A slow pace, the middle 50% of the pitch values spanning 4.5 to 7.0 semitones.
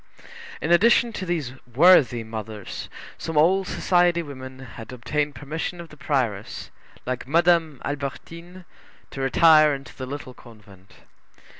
Yes: slow, 130 wpm; average, 5.0 semitones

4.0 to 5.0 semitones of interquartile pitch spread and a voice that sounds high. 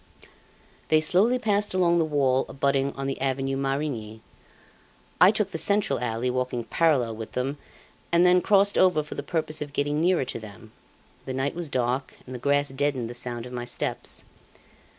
No: average, 4.7 semitones; medium, 140 Hz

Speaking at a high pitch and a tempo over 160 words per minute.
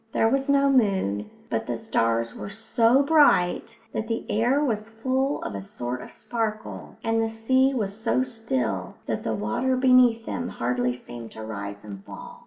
Yes: high, 220 Hz; average, 180 wpm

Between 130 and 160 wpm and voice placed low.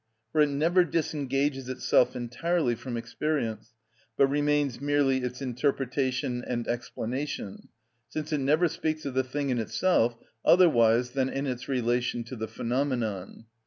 Yes: average, 140 wpm; low, 130 Hz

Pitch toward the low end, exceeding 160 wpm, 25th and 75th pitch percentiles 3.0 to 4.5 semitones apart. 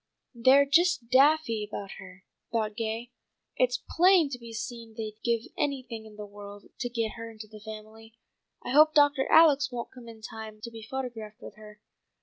No: high, 230 Hz; average, 180 wpm; average, 3.4 semitones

